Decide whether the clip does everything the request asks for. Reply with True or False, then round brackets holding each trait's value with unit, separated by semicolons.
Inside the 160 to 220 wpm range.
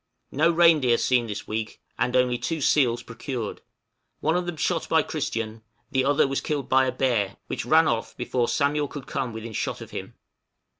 True (190 wpm)